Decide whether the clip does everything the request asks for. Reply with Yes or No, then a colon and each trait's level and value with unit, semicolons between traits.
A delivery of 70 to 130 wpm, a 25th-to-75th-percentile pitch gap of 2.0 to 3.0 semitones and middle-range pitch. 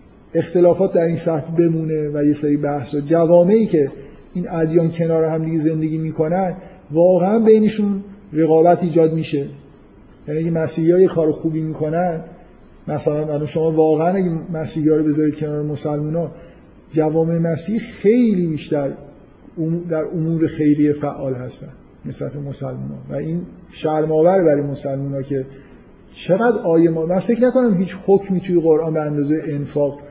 No: average, 150 wpm; narrow, 2.6 semitones; medium, 160 Hz